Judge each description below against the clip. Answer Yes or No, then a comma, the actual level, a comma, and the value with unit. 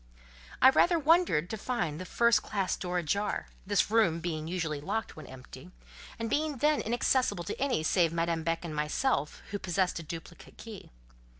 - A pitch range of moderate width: No, wide, 6.1 semitones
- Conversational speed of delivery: Yes, average, 175 wpm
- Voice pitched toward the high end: No, medium, 180 Hz